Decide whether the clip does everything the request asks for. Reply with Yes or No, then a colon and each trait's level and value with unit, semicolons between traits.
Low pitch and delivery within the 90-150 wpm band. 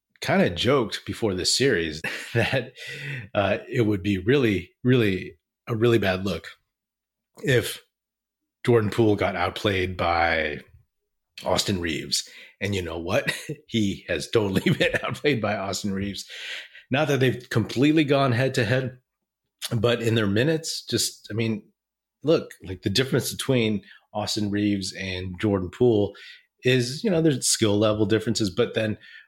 Yes: low, 110 Hz; average, 145 wpm